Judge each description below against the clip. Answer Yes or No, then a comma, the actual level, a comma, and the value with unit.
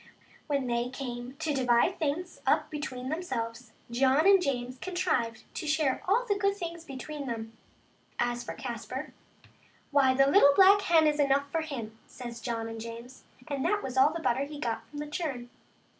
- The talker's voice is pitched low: No, very high, 275 Hz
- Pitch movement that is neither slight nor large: Yes, average, 4.6 semitones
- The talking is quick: No, average, 190 wpm